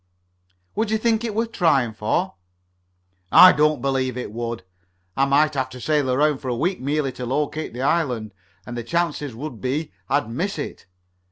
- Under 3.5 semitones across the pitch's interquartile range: No, average, 4.2 semitones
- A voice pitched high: No, medium, 140 Hz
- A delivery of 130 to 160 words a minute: No, average, 180 wpm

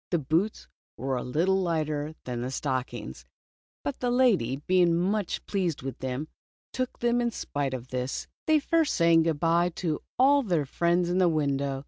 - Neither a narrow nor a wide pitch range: No, wide, 5.7 semitones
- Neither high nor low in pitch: Yes, medium, 165 Hz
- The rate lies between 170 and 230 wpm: Yes, average, 175 wpm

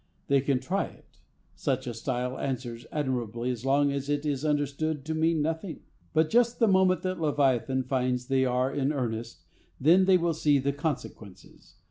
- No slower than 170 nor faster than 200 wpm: Yes, average, 175 wpm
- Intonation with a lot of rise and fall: No, average, 3.7 semitones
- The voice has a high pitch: No, medium, 140 Hz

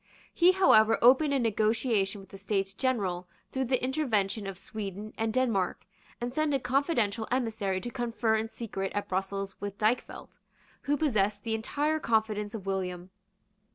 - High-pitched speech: Yes, high, 220 Hz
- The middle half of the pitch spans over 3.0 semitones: Yes, average, 4.3 semitones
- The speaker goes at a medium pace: Yes, average, 155 wpm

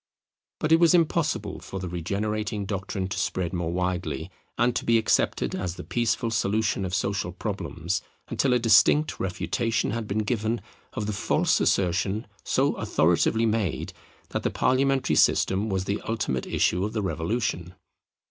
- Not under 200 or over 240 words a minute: No, average, 155 wpm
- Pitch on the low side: Yes, low, 100 Hz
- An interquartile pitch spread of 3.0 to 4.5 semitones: Yes, average, 3.8 semitones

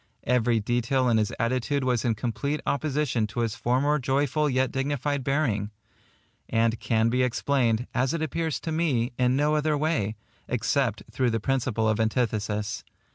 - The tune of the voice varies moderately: Yes, average, 3.8 semitones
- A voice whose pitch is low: Yes, low, 125 Hz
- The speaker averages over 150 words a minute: Yes, average, 160 wpm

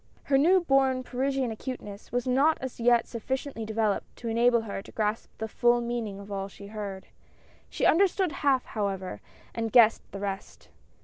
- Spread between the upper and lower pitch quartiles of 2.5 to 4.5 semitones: Yes, average, 4.0 semitones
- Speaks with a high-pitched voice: Yes, high, 235 Hz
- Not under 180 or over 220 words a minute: No, average, 170 wpm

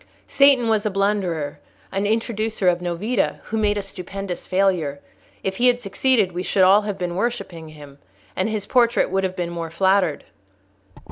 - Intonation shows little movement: No, average, 3.5 semitones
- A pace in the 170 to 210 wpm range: Yes, average, 175 wpm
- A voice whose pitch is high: Yes, high, 195 Hz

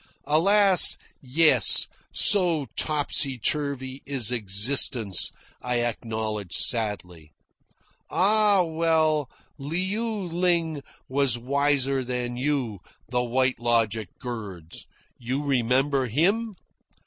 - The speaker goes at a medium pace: No, slow, 90 wpm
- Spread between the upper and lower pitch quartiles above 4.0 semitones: Yes, average, 5.2 semitones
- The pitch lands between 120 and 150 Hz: Yes, low, 135 Hz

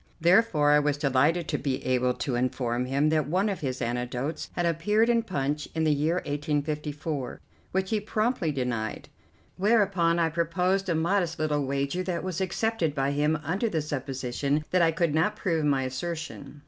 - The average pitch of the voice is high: No, medium, 155 Hz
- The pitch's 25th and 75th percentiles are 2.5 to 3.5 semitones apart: No, average, 4.3 semitones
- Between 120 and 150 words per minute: No, average, 175 wpm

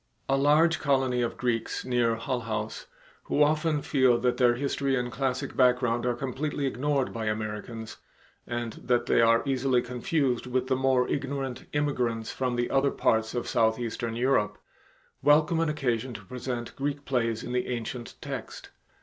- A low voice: Yes, low, 125 Hz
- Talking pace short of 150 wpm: No, average, 160 wpm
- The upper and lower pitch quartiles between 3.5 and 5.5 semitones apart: No, narrow, 2.6 semitones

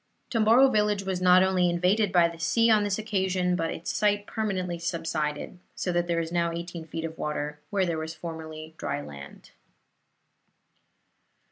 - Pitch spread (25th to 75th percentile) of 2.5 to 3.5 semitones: Yes, average, 3.2 semitones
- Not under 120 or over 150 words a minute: No, average, 165 wpm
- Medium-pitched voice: Yes, medium, 175 Hz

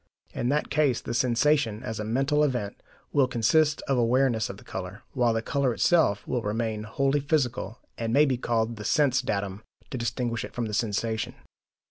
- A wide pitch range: No, average, 3.6 semitones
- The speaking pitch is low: Yes, low, 120 Hz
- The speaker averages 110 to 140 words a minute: No, average, 185 wpm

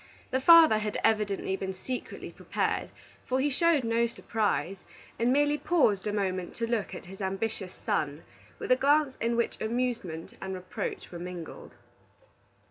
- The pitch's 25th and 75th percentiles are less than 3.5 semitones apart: No, average, 5.2 semitones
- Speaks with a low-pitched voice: No, high, 220 Hz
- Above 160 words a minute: No, average, 155 wpm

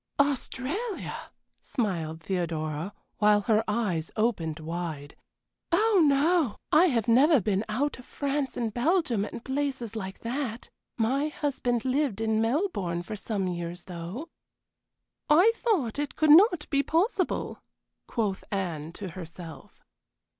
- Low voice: No, high, 230 Hz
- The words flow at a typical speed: No, slow, 125 wpm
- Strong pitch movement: Yes, wide, 7.6 semitones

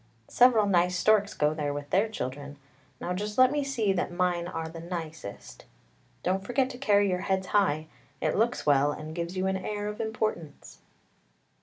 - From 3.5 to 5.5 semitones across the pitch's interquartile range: Yes, average, 4.6 semitones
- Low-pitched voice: No, medium, 185 Hz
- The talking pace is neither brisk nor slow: Yes, average, 180 wpm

